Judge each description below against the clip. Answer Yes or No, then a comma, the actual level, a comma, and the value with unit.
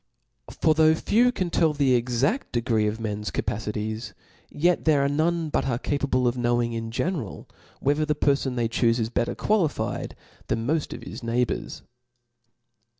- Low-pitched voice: Yes, low, 130 Hz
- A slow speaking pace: No, average, 165 wpm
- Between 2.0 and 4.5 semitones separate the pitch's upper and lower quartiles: No, average, 5.1 semitones